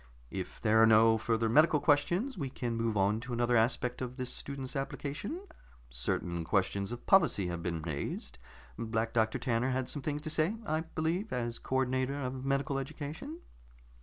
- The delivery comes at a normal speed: Yes, average, 175 wpm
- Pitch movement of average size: Yes, average, 4.5 semitones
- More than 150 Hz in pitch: No, low, 125 Hz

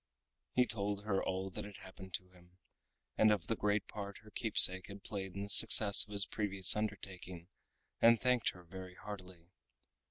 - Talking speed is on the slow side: No, average, 180 wpm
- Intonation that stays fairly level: Yes, narrow, 2.2 semitones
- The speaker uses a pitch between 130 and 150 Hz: No, low, 100 Hz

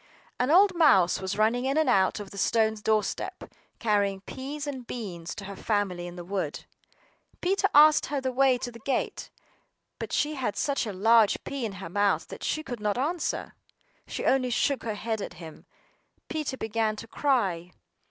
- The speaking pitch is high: Yes, high, 225 Hz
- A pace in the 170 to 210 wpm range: Yes, average, 185 wpm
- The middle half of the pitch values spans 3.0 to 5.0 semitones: No, wide, 5.4 semitones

